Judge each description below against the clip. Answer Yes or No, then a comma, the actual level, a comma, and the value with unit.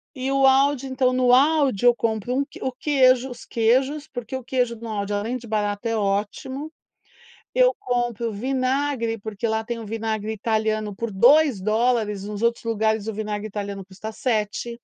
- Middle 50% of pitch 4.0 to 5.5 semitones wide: No, average, 3.3 semitones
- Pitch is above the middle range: Yes, high, 230 Hz